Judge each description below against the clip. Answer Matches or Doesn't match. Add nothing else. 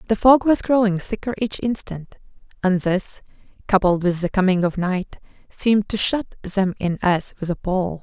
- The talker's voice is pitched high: Matches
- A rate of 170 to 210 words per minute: Matches